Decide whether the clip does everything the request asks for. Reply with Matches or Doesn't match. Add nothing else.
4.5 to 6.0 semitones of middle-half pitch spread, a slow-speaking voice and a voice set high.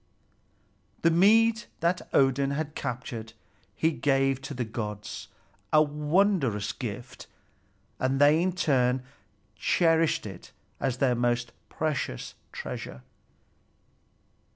Doesn't match